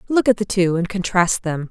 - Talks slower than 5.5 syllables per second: Yes, 5.2 syllables/s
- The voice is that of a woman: Yes, female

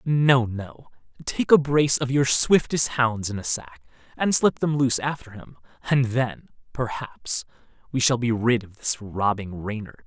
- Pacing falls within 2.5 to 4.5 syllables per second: Yes, 4.4 syllables/s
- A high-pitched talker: No, low, 120 Hz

